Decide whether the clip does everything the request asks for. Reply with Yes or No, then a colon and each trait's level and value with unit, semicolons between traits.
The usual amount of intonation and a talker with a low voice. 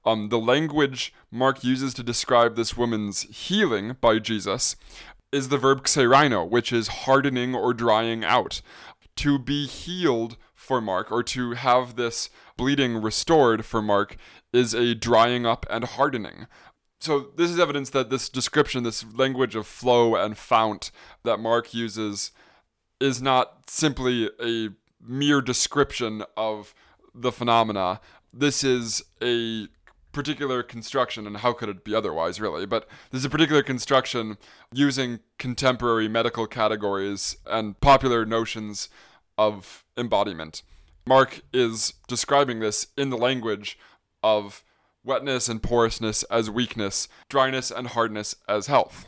Yes: average, 3.1 semitones; low, 120 Hz